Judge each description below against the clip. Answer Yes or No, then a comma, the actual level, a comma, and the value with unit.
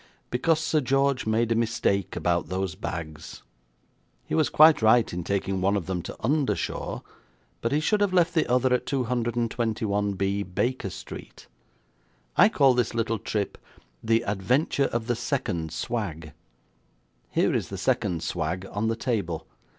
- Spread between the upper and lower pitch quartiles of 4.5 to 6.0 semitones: Yes, average, 5.0 semitones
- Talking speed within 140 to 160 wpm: Yes, average, 150 wpm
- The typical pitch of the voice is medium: No, low, 115 Hz